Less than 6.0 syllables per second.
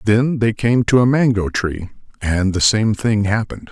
Yes: 4.6 syllables/s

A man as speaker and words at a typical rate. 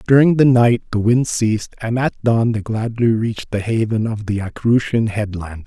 Yes: male; average, 190 wpm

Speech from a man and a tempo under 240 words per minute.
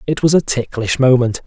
Yes: male; fast, 205 wpm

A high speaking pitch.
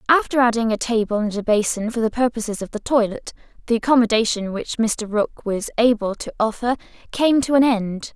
Yes: high, 225 Hz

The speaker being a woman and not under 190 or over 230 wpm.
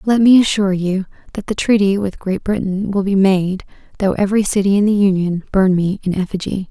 Yes: female; fast, 205 wpm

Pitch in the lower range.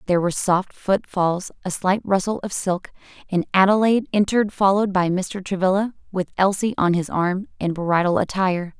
No: high, 190 Hz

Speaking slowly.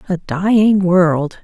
Yes: slow, 125 wpm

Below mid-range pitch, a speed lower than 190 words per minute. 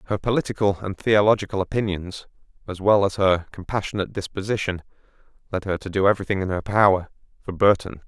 Yes: low, 100 Hz; average, 155 wpm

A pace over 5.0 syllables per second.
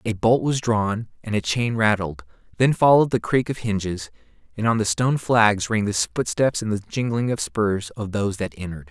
Yes: 5.2 syllables/s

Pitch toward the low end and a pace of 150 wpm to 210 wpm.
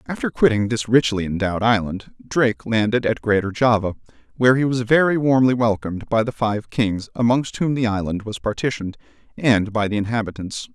Yes: low, 115 Hz; average, 175 wpm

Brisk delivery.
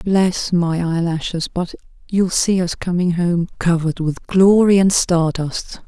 No: average, 155 wpm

